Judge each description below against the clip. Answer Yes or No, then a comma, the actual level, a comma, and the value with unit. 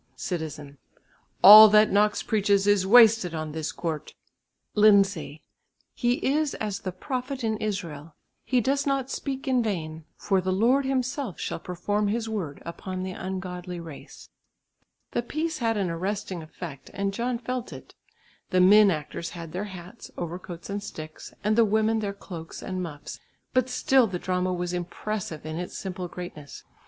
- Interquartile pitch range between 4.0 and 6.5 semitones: Yes, average, 4.4 semitones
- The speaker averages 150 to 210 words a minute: Yes, average, 160 wpm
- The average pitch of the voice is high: Yes, high, 195 Hz